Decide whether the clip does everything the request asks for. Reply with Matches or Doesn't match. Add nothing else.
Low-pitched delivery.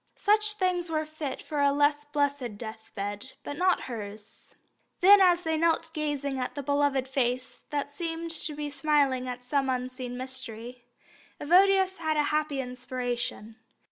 Doesn't match